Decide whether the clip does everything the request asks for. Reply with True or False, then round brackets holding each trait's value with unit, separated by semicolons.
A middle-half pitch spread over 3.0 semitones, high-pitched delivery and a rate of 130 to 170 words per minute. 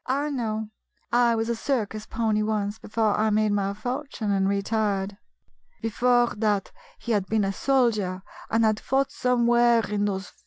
False (2.6 semitones; 220 Hz; 165 wpm)